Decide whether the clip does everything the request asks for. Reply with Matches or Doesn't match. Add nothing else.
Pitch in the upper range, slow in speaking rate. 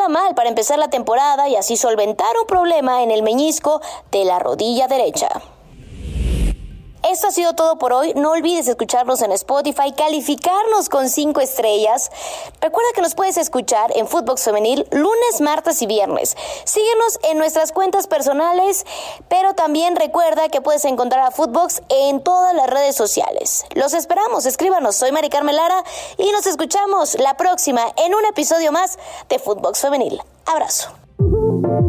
Doesn't match